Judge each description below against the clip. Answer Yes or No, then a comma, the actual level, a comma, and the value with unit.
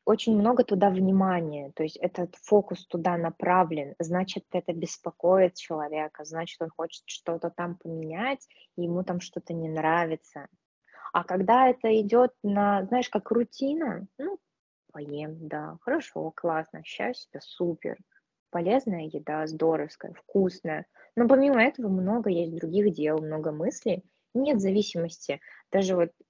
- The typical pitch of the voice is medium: Yes, medium, 180 Hz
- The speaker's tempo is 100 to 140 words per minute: Yes, average, 130 wpm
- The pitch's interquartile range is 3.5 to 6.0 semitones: Yes, average, 4.6 semitones